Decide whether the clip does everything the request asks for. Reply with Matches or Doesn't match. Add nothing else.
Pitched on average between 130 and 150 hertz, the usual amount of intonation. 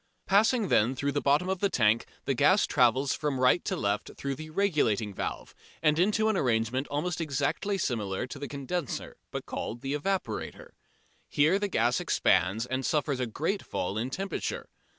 Doesn't match